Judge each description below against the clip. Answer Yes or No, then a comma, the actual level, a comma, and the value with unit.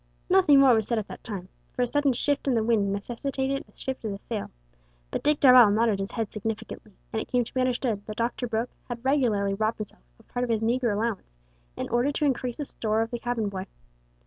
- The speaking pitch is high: Yes, high, 235 Hz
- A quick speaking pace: Yes, fast, 235 wpm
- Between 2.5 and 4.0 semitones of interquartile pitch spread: Yes, average, 3.0 semitones